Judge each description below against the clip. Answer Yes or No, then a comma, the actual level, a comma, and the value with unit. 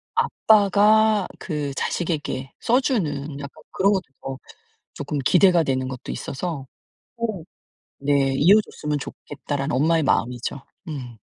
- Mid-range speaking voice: Yes, medium, 150 Hz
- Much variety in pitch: Yes, wide, 6.0 semitones